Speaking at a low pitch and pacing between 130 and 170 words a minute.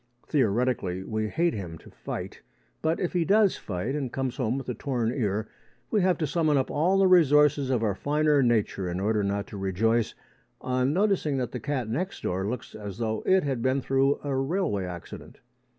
No: low, 130 Hz; average, 200 wpm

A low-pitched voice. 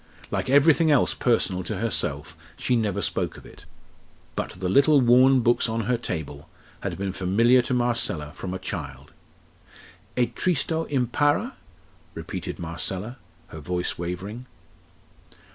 Yes: low, 110 Hz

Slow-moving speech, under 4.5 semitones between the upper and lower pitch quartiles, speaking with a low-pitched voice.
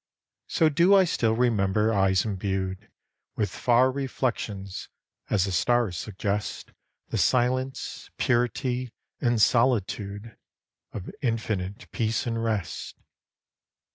Yes: slow, 105 wpm; average, 3.9 semitones; low, 115 Hz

